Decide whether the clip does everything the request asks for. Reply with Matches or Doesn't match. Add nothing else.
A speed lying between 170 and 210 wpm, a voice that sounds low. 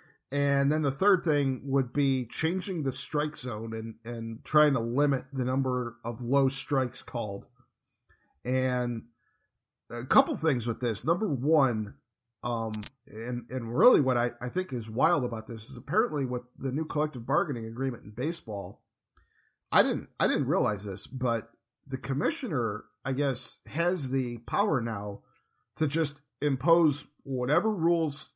Doesn't match